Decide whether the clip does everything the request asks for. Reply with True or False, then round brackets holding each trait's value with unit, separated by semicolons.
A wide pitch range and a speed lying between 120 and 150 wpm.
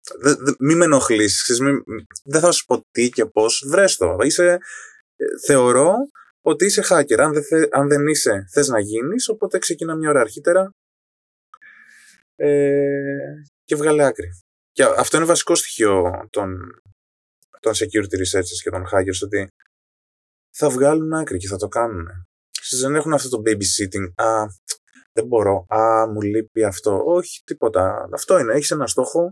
False (8.0 semitones; 165 wpm)